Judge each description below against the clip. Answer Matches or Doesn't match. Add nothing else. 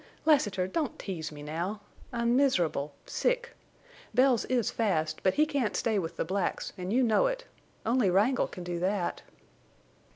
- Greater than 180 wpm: Doesn't match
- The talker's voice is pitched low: Doesn't match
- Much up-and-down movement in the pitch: Matches